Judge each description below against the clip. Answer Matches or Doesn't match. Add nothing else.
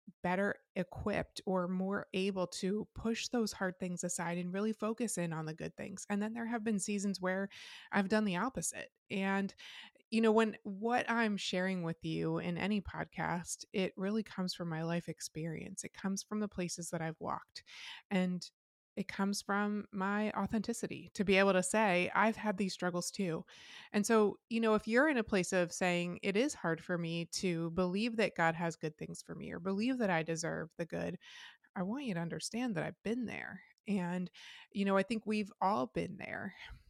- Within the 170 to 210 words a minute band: Matches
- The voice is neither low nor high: Doesn't match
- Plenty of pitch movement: Doesn't match